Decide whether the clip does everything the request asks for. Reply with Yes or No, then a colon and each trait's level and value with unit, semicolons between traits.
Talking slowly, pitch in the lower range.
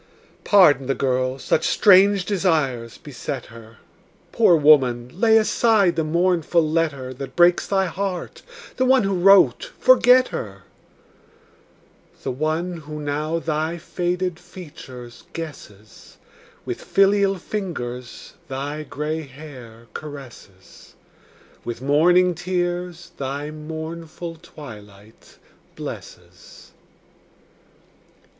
No: slow, 100 wpm; medium, 155 Hz